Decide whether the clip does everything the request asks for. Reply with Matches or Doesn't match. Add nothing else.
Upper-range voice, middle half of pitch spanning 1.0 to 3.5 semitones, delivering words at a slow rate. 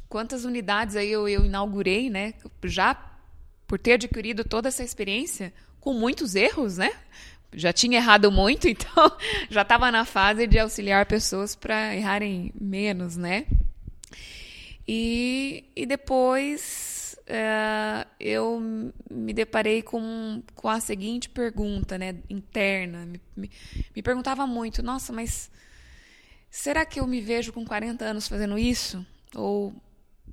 Doesn't match